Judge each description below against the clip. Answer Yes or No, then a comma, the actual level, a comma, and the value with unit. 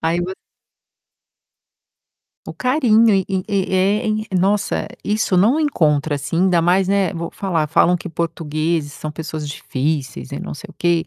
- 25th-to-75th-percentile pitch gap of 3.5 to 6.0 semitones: Yes, average, 3.9 semitones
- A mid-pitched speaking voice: Yes, medium, 175 Hz